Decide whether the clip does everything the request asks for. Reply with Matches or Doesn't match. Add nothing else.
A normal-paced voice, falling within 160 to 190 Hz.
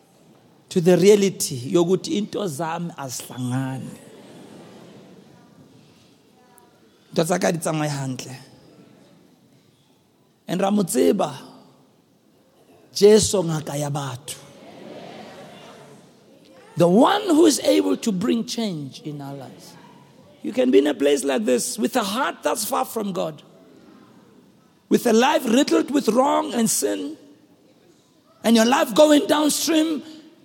Doesn't match